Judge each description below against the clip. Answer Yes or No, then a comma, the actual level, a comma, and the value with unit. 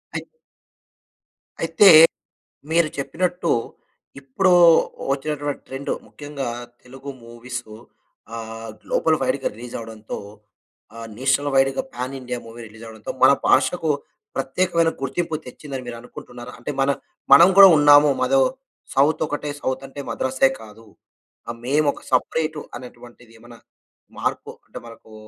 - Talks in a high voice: No, low, 135 Hz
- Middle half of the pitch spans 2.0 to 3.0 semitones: No, average, 3.5 semitones